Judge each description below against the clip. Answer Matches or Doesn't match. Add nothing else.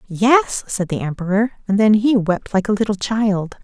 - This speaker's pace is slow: Doesn't match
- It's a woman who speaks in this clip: Matches